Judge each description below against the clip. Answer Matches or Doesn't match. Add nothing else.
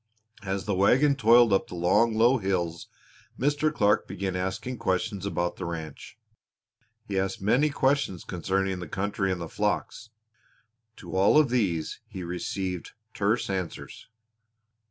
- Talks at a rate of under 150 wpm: Matches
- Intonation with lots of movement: Doesn't match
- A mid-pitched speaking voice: Doesn't match